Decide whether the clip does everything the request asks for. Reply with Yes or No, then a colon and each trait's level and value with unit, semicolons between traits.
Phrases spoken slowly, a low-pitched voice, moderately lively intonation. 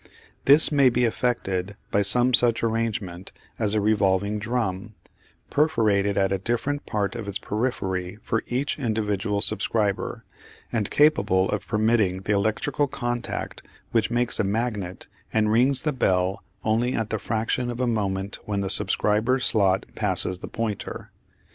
No: average, 150 wpm; low, 110 Hz; average, 3.4 semitones